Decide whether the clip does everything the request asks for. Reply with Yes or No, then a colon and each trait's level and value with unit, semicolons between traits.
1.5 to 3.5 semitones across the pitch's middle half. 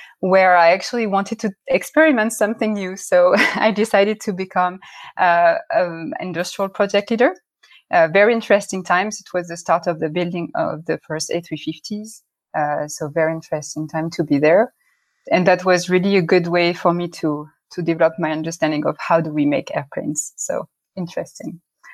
No: average, 4.2 semitones